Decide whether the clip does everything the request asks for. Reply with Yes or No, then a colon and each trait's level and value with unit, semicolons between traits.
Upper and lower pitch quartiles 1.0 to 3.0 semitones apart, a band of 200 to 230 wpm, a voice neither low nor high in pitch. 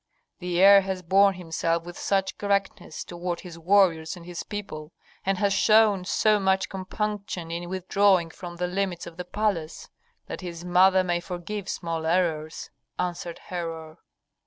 No: narrow, 2.5 semitones; average, 155 wpm; medium, 180 Hz